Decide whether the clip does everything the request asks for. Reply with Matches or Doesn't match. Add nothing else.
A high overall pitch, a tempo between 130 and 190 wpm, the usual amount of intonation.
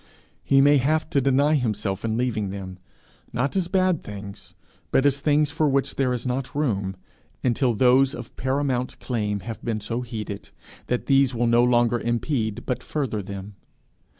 Doesn't match